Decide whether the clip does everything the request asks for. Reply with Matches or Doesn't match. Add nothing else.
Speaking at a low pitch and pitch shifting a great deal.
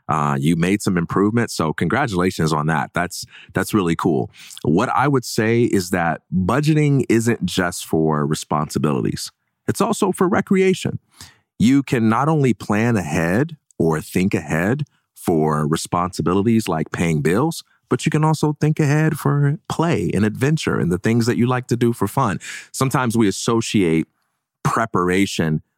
Matches